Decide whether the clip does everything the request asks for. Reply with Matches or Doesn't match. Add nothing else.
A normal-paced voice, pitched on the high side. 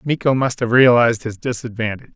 Doesn't match